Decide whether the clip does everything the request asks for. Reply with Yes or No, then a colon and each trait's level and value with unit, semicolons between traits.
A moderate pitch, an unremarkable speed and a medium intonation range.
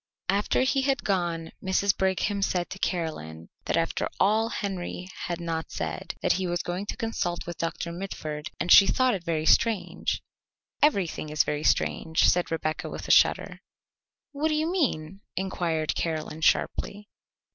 Yes: medium, 180 Hz; average, 160 wpm; average, 3.8 semitones